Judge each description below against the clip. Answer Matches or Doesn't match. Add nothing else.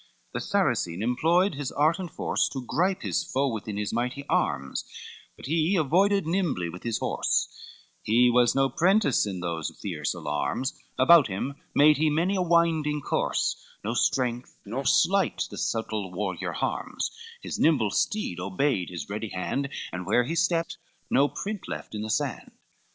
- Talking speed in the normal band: Matches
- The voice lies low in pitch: Matches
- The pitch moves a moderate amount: Doesn't match